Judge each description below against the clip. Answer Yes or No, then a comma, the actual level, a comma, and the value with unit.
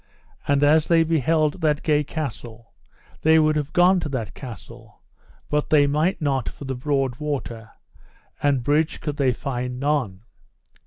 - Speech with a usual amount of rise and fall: Yes, average, 3.1 semitones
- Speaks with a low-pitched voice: No, medium, 145 Hz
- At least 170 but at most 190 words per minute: No, average, 155 wpm